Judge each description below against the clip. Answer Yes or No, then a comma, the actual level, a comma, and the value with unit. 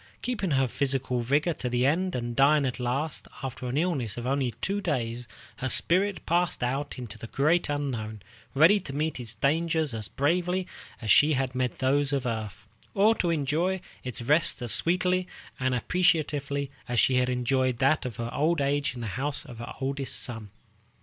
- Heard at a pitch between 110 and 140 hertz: Yes, low, 135 Hz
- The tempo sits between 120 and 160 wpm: No, average, 185 wpm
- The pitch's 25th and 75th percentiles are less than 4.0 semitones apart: No, average, 4.4 semitones